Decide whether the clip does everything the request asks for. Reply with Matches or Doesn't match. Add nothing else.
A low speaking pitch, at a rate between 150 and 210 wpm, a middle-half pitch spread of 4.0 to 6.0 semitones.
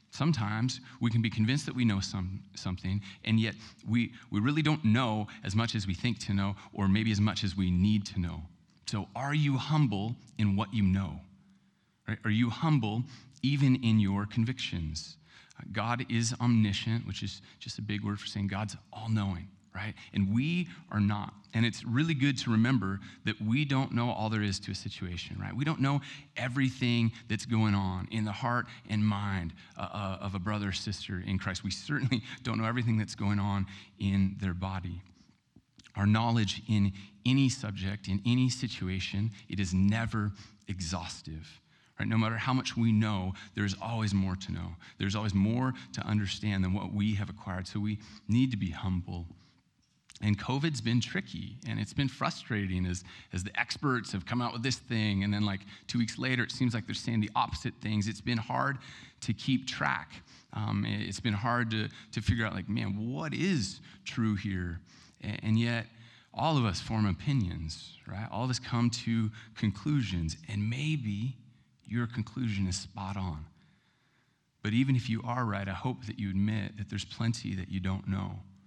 Doesn't match